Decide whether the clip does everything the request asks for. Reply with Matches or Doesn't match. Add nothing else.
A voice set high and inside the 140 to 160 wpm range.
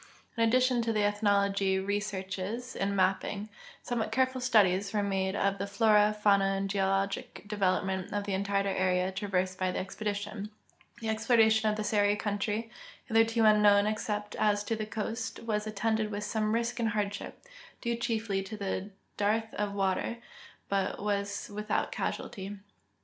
Matches